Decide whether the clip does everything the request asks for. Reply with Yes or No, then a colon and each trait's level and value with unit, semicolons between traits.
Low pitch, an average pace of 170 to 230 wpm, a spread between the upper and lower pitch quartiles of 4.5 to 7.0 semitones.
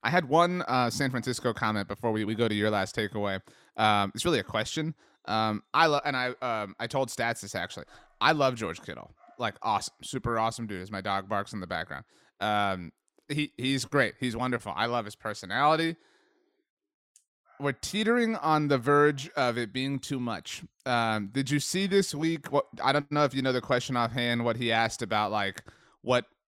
Yes: low, 120 Hz; average, 200 wpm; average, 5.2 semitones